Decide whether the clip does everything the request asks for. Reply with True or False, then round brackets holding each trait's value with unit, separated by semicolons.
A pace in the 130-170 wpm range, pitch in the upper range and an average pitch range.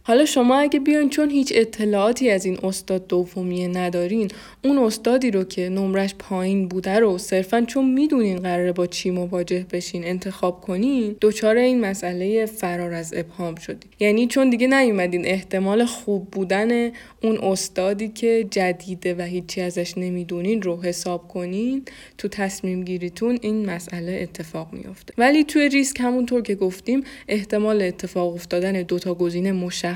True (150 wpm; 195 Hz; 4.3 semitones)